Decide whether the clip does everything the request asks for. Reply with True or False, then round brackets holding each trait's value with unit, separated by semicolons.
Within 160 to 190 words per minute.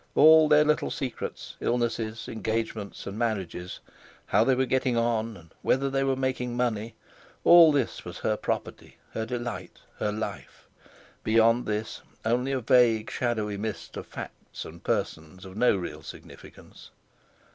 False (145 wpm)